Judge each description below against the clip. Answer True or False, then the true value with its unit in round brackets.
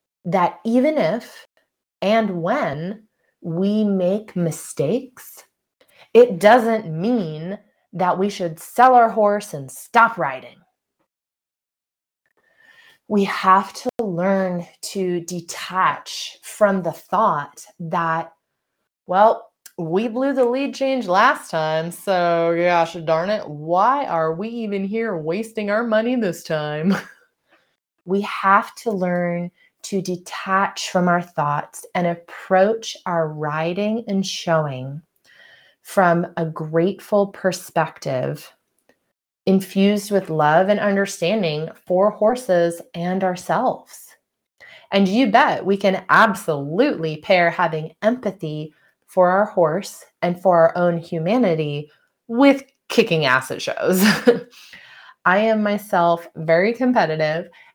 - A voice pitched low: False (190 Hz)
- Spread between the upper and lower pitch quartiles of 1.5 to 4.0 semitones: False (4.4 semitones)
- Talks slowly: True (110 wpm)